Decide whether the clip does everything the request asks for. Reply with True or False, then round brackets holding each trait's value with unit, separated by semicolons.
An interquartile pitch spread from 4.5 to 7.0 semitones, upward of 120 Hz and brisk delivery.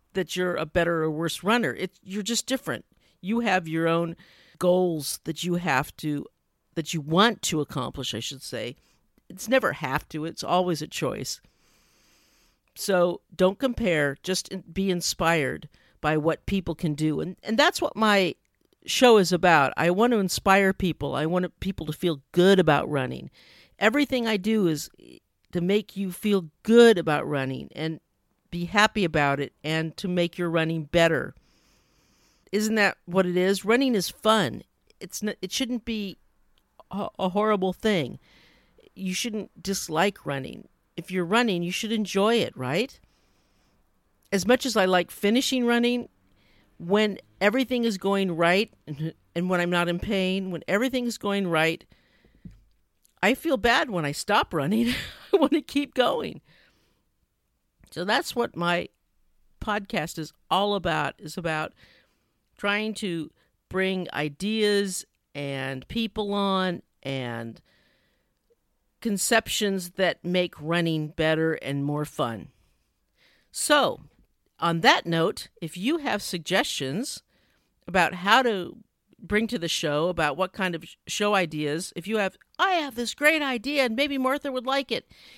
False (4.8 semitones; 185 Hz; 150 wpm)